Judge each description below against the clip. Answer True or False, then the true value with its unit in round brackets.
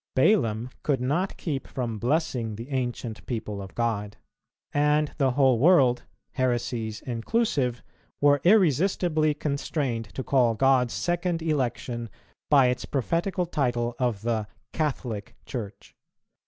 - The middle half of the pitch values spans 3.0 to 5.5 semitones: True (4.2 semitones)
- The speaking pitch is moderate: False (130 Hz)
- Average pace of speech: False (120 wpm)